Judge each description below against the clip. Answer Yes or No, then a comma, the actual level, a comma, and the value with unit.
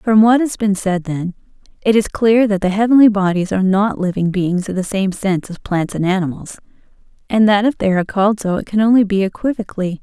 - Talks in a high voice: Yes, high, 200 Hz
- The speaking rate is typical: No, fast, 220 wpm